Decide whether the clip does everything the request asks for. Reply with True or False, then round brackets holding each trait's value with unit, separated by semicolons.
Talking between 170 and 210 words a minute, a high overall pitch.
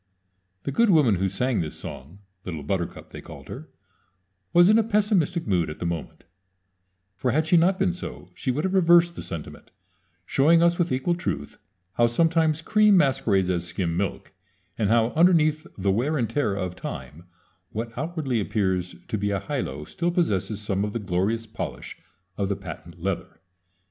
False (180 wpm; 115 Hz)